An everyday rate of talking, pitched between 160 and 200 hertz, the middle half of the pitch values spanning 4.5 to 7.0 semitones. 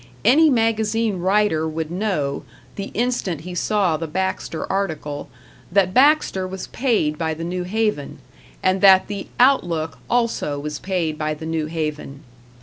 Yes: average, 145 wpm; medium, 185 Hz; average, 5.1 semitones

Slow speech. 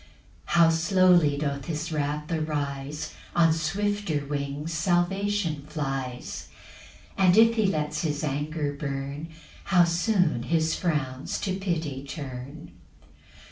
Yes: slow, 115 wpm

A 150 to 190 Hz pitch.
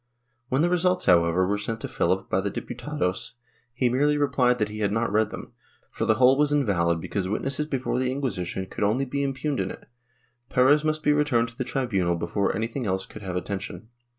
No: low, 120 Hz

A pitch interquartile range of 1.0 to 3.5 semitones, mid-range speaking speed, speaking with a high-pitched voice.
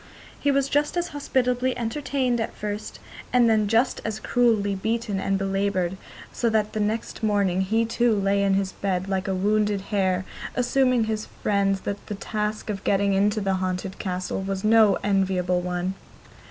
Yes: average, 2.8 semitones; average, 165 wpm; high, 205 Hz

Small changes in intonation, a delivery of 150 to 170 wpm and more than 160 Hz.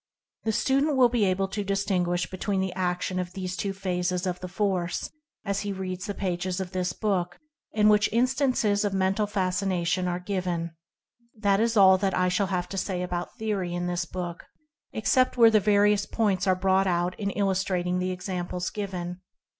No: narrow, 2.2 semitones; average, 185 wpm; high, 190 Hz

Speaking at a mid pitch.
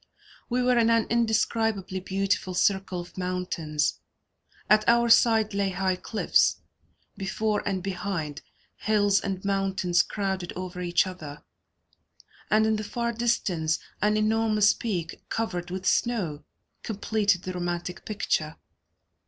No: high, 195 Hz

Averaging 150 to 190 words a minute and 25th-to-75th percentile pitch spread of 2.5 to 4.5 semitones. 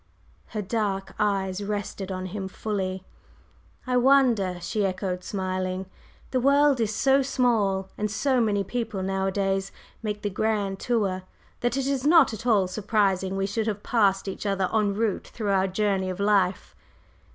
Yes: average, 160 wpm; average, 2.8 semitones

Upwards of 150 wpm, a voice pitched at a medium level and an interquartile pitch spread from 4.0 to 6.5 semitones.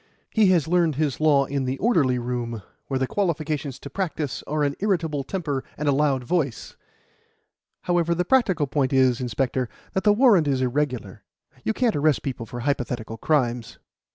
Yes: average, 170 wpm; medium, 145 Hz; average, 4.7 semitones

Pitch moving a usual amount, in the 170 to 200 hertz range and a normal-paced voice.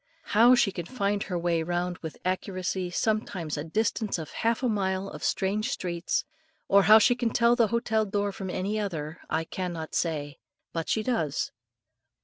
Yes: average, 4.0 semitones; high, 190 Hz; average, 175 wpm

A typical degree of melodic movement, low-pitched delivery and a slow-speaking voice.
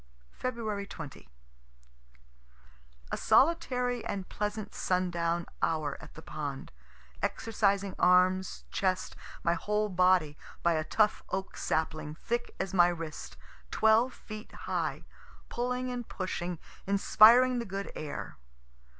No: average, 4.4 semitones; high, 195 Hz; slow, 115 wpm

